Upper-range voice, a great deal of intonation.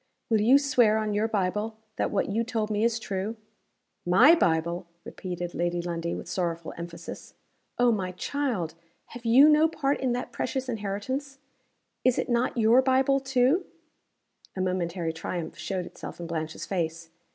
Yes: high, 210 Hz; wide, 6.4 semitones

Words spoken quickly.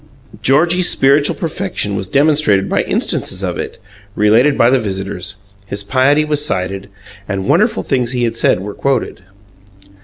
No: average, 150 wpm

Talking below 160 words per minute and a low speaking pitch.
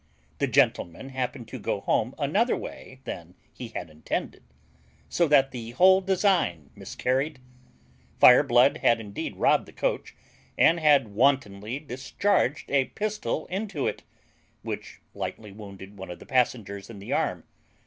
Yes: average, 140 wpm; low, 130 Hz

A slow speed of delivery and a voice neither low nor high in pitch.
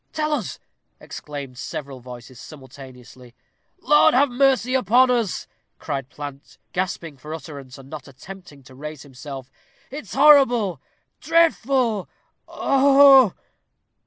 Yes: slow, 115 wpm; medium, 160 Hz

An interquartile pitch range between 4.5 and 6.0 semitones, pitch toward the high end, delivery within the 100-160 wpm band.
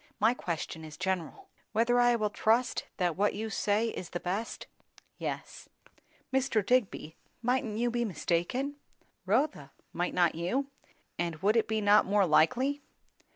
Yes: wide, 5.4 semitones; high, 215 Hz; average, 150 wpm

